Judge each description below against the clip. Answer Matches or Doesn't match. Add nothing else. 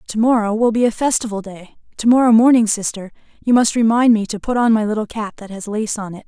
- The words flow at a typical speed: Doesn't match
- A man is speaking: Doesn't match